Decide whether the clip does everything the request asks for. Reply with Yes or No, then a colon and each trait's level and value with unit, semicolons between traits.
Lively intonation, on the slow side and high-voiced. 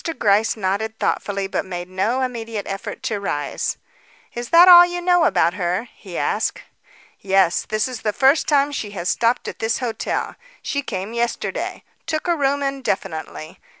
No: wide, 5.9 semitones; average, 165 wpm; high, 220 Hz